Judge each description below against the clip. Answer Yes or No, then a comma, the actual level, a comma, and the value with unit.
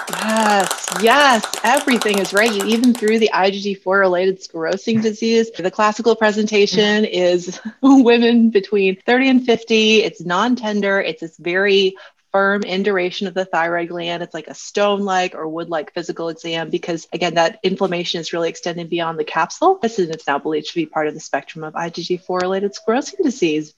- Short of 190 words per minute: Yes, average, 160 wpm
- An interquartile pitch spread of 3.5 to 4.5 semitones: Yes, average, 3.9 semitones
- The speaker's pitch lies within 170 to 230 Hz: Yes, high, 190 Hz